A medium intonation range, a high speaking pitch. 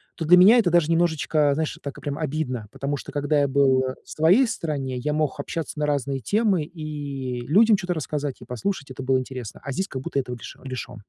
No: average, 3.7 semitones; medium, 145 Hz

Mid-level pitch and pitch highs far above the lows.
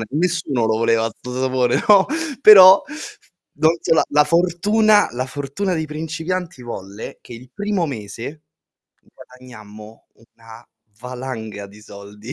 No: low, 130 Hz; wide, 6.9 semitones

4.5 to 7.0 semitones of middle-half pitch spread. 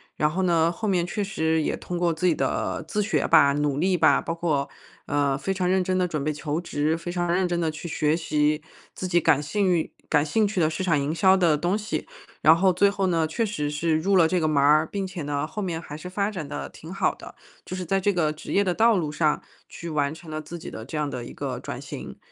No: average, 3.4 semitones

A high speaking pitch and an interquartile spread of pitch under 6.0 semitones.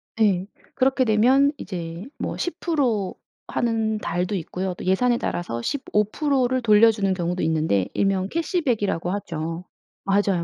Yes: high, 205 Hz; wide, 5.5 semitones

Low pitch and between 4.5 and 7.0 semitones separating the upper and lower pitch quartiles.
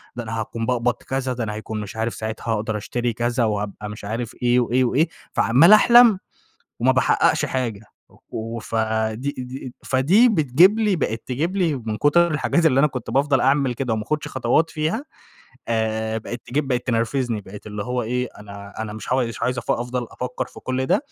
No: low, 125 Hz; average, 3.6 semitones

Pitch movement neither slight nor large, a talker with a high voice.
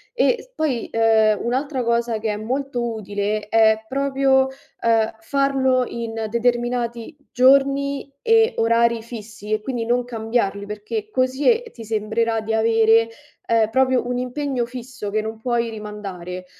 Yes: average, 3.1 semitones; high, 235 Hz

